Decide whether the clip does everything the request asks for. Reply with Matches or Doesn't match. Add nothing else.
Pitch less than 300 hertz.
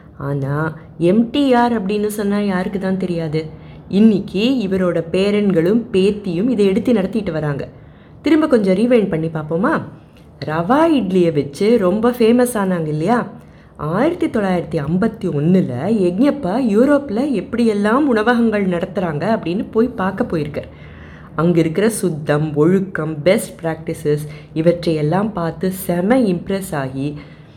Matches